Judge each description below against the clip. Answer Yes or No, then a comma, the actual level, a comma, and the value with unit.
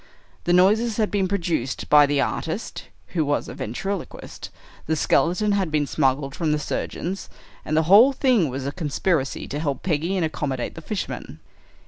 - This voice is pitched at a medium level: Yes, medium, 160 Hz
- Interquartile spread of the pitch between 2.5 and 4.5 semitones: No, average, 5.0 semitones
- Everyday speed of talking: Yes, average, 170 wpm